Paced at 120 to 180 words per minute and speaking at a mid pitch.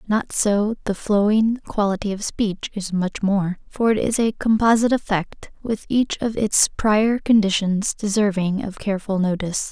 No: average, 155 wpm; high, 205 Hz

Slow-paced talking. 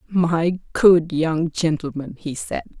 Yes: slow, 130 wpm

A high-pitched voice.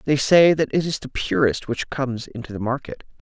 No: low, 135 Hz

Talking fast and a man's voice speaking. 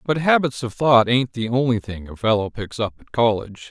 Yes: fast, 225 wpm; male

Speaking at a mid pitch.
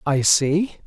Yes: medium, 160 Hz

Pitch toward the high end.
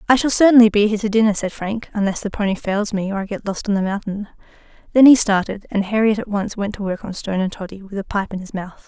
Yes: high, 205 Hz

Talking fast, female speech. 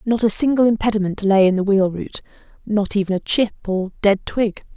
No: average, 190 wpm; female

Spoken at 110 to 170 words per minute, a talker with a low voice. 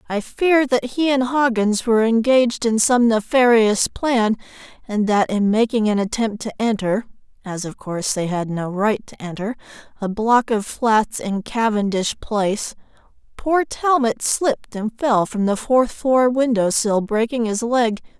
No: average, 160 wpm; high, 225 Hz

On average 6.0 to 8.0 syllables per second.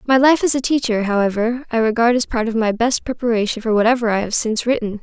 Yes: 6.5 syllables/s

